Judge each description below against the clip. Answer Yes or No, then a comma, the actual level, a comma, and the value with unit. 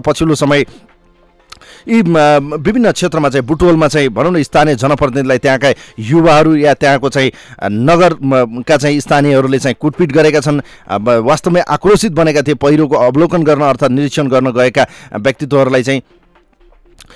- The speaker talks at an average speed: No, slow, 130 wpm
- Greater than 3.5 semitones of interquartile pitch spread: No, average, 2.8 semitones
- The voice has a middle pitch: Yes, medium, 145 Hz